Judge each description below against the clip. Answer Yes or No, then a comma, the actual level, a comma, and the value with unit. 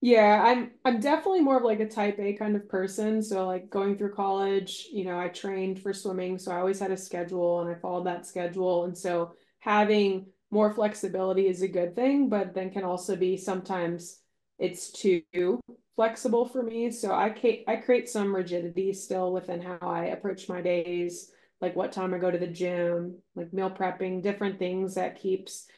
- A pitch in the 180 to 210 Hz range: Yes, high, 190 Hz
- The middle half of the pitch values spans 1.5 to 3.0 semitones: Yes, narrow, 2.5 semitones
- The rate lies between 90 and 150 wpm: No, average, 195 wpm